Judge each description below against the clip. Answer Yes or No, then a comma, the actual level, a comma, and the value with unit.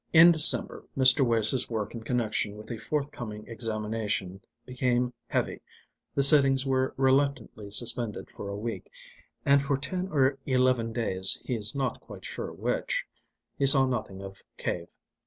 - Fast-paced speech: No, average, 150 wpm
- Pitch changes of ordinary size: Yes, average, 4.0 semitones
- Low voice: Yes, low, 125 Hz